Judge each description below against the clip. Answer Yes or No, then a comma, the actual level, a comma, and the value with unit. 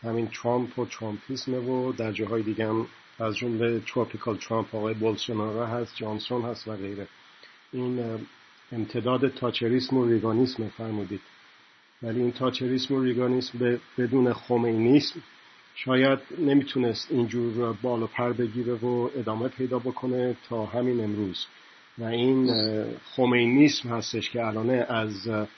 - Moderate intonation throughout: No, narrow, 2.1 semitones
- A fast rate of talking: No, average, 125 wpm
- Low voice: Yes, low, 120 Hz